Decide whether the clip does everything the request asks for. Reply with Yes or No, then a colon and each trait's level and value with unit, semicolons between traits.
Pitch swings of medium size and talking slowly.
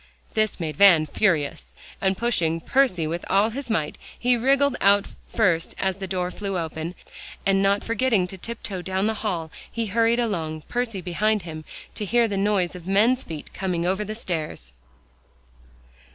No: average, 4.4 semitones; average, 165 wpm